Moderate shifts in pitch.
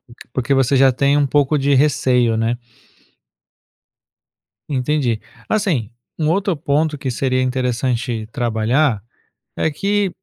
Yes: average, 3.5 semitones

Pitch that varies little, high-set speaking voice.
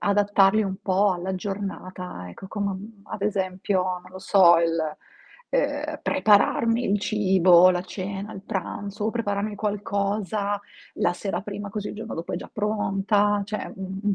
Yes: narrow, 1.7 semitones; high, 200 Hz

